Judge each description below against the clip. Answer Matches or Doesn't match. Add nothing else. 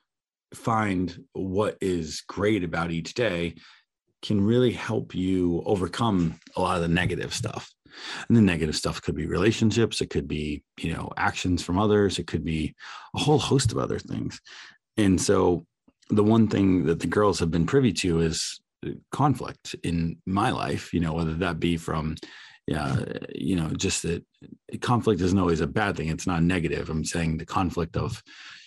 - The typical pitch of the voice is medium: Doesn't match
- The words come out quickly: Doesn't match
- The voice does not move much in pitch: Doesn't match